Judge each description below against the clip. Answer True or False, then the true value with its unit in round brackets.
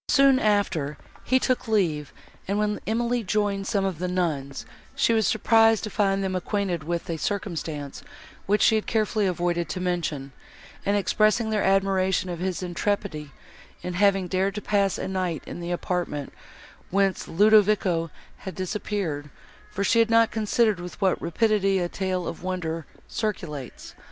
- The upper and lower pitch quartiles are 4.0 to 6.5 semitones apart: False (3.3 semitones)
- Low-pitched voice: False (190 Hz)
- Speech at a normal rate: True (160 wpm)